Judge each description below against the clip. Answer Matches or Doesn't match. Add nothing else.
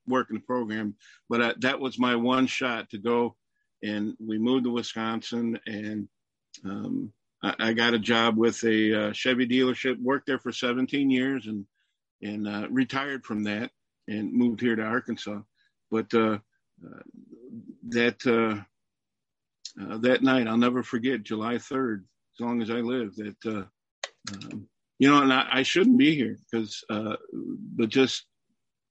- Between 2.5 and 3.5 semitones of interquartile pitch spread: Matches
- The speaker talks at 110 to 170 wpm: Matches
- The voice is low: Matches